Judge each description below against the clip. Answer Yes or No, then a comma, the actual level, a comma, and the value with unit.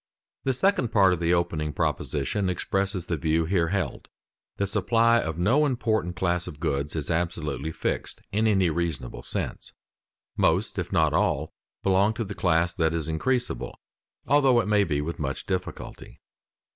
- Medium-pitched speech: No, very low, 90 Hz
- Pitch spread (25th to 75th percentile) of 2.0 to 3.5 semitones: No, average, 4.7 semitones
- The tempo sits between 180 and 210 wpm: No, average, 160 wpm